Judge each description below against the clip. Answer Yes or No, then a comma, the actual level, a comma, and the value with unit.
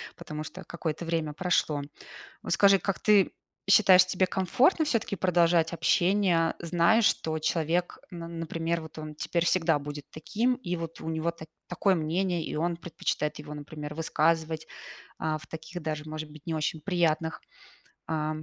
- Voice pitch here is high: No, medium, 165 Hz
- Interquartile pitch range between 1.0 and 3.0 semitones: Yes, narrow, 2.4 semitones